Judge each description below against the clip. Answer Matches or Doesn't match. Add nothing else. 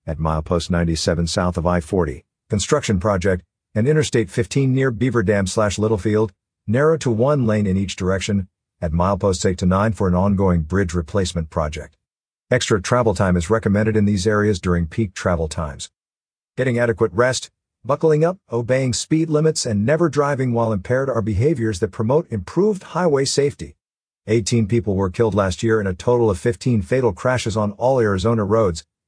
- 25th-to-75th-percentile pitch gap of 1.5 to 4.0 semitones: Doesn't match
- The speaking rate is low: Doesn't match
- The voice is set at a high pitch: Doesn't match